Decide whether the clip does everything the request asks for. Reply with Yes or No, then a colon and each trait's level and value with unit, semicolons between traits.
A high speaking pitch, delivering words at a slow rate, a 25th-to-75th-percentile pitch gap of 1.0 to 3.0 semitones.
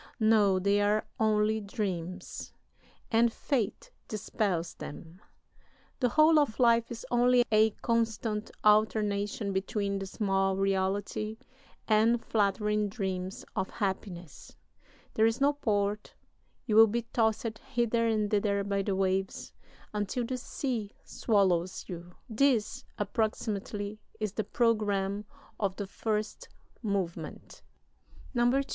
Yes: high, 210 Hz; slow, 115 wpm; narrow, 2.5 semitones